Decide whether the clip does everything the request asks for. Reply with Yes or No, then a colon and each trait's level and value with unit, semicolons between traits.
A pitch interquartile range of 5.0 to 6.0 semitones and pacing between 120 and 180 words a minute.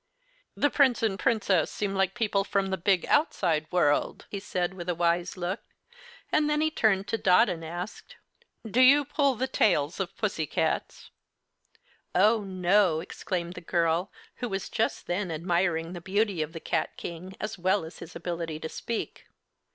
No: average, 3.9 semitones; average, 170 wpm